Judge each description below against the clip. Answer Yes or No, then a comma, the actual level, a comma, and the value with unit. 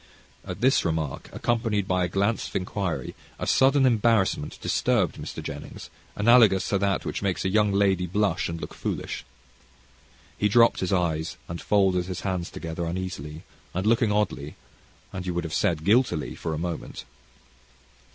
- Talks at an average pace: Yes, average, 160 wpm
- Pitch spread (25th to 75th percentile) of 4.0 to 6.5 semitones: No, average, 3.4 semitones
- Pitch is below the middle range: Yes, very low, 95 Hz